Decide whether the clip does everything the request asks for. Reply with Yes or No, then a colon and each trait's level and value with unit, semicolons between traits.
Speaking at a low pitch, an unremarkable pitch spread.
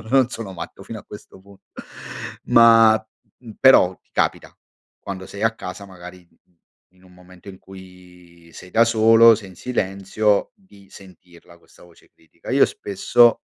Yes: very low, 95 Hz; average, 3.6 semitones